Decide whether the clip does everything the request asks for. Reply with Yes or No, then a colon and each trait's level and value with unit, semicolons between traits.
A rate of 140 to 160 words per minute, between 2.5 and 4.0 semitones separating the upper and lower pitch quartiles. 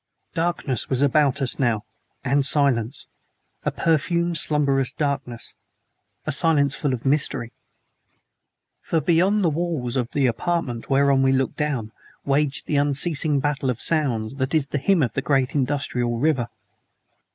Yes: average, 145 wpm; average, 2.9 semitones